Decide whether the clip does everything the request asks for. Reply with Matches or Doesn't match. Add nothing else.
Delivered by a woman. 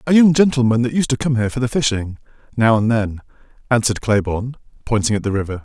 Doesn't match